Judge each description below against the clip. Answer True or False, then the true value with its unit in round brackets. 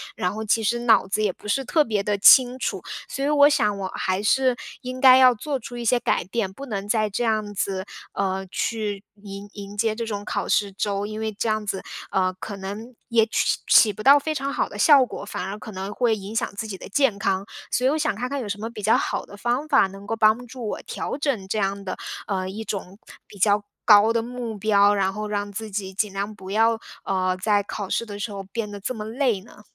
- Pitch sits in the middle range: False (215 Hz)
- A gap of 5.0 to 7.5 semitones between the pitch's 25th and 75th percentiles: False (3.1 semitones)